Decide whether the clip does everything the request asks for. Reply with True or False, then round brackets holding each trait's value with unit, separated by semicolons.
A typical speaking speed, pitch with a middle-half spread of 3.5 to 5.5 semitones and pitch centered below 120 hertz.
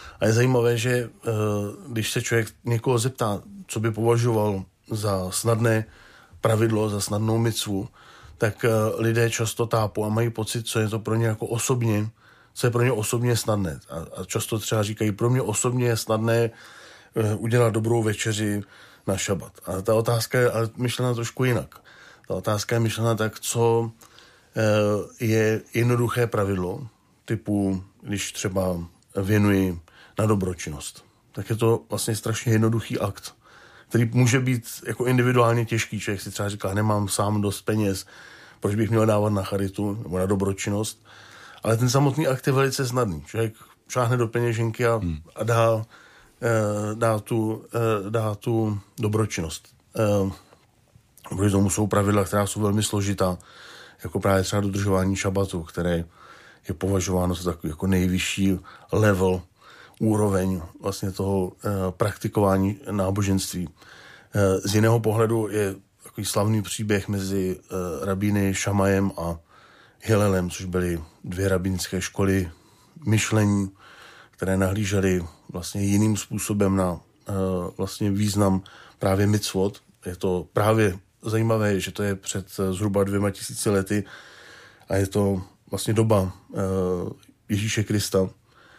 False (135 wpm; 2.8 semitones; 105 Hz)